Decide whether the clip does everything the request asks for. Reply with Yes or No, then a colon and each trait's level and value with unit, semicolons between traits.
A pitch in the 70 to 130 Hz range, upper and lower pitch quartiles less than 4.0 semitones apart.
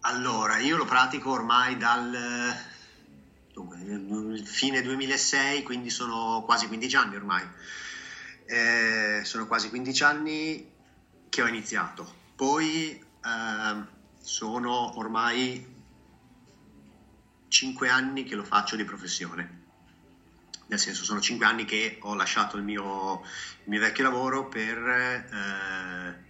No: low, 110 Hz; average, 5.2 semitones